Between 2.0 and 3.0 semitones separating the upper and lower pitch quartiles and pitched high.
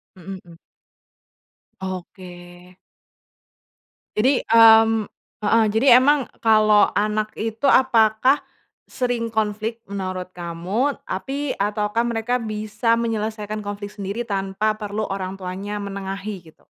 Yes: narrow, 2.5 semitones; high, 215 Hz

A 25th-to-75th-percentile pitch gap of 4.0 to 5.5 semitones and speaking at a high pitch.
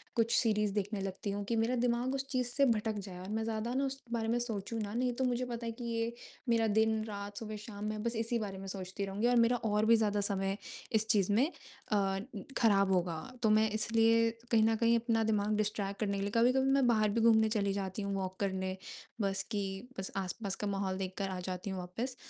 No: narrow, 2.6 semitones; high, 215 Hz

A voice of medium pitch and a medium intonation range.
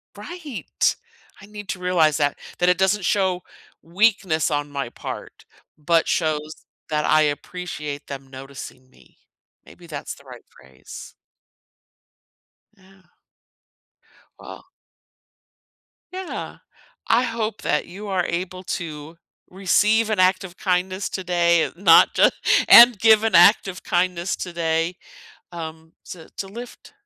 Yes: medium, 180 Hz; average, 3.7 semitones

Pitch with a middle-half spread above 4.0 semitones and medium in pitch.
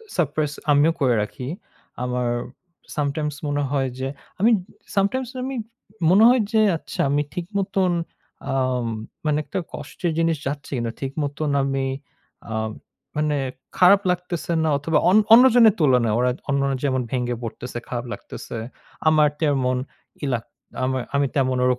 Yes: average, 4.7 semitones; medium, 145 Hz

